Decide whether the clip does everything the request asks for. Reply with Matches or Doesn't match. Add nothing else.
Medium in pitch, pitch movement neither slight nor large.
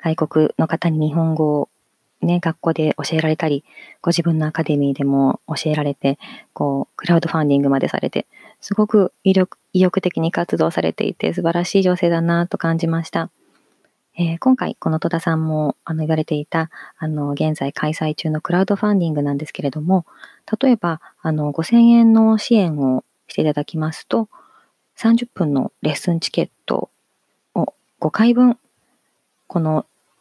Matches